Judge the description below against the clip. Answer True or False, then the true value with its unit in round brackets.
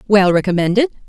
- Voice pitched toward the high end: True (200 Hz)